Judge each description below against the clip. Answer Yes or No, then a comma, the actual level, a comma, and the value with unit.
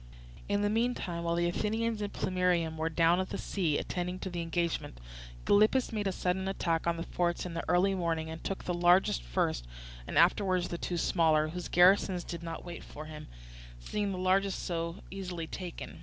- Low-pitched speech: No, medium, 175 Hz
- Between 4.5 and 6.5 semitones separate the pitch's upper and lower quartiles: No, narrow, 2.4 semitones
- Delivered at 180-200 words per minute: Yes, average, 195 wpm